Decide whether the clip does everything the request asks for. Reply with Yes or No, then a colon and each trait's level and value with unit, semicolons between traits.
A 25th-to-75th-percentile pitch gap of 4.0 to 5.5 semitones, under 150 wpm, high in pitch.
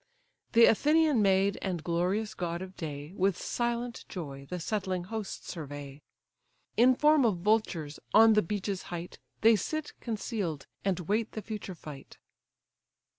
Yes: average, 4.7 semitones; average, 140 wpm; high, 195 Hz